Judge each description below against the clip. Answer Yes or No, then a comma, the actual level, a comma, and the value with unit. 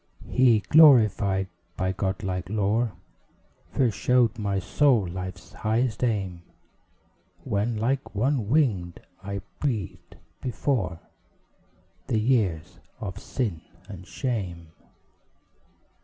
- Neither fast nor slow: No, slow, 95 wpm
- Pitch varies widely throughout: No, average, 4.6 semitones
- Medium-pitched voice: No, low, 105 Hz